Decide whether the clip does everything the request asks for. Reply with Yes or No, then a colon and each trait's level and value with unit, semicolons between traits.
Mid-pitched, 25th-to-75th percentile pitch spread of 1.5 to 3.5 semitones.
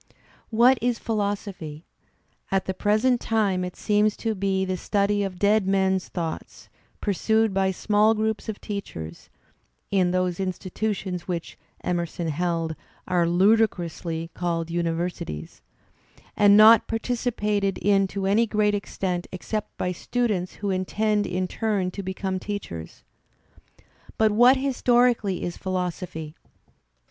No: high, 195 Hz; average, 3.1 semitones